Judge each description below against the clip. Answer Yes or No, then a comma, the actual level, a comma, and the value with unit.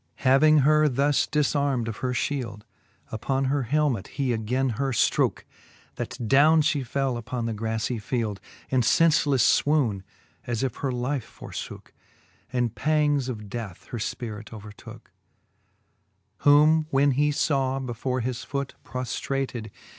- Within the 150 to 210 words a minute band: No, average, 140 wpm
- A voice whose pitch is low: Yes, low, 130 Hz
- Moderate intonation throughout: Yes, average, 3.6 semitones